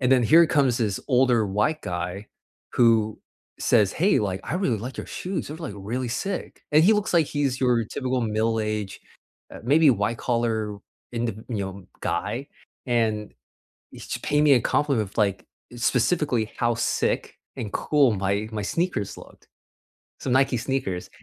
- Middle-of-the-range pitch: No, low, 120 Hz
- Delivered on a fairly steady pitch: No, average, 4.5 semitones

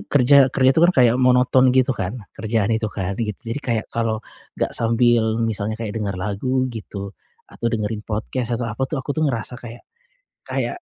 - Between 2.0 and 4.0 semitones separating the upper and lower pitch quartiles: Yes, average, 2.9 semitones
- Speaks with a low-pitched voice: Yes, low, 115 Hz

